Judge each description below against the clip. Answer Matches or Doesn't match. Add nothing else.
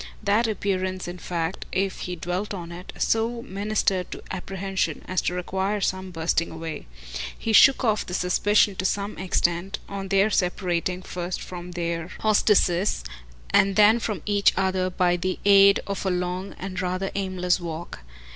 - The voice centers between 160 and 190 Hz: Matches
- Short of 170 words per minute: Matches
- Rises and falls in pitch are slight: Matches